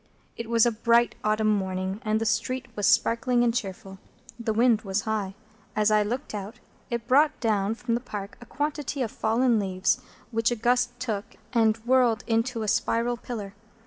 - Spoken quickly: No, average, 180 wpm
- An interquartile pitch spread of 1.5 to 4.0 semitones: Yes, narrow, 2.4 semitones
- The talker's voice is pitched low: No, high, 225 Hz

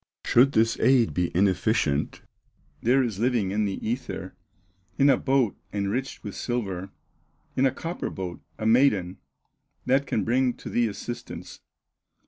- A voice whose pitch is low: Yes, low, 115 Hz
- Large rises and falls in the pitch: No, average, 4.7 semitones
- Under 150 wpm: Yes, average, 140 wpm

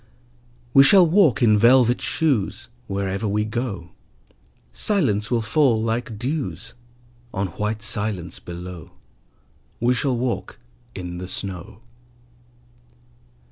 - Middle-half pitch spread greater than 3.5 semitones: Yes, average, 4.4 semitones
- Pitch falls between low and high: No, low, 110 Hz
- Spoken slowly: Yes, slow, 105 wpm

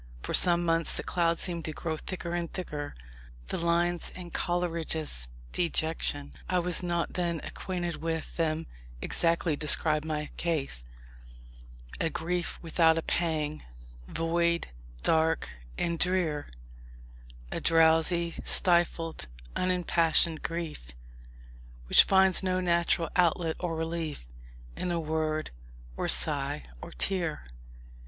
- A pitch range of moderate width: No, narrow, 1.5 semitones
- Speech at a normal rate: No, slow, 115 wpm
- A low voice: No, medium, 165 Hz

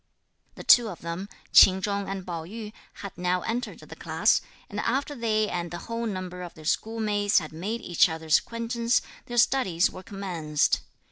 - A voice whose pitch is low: No, high, 200 Hz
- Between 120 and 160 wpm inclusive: No, average, 180 wpm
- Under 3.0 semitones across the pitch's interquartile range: No, average, 4.6 semitones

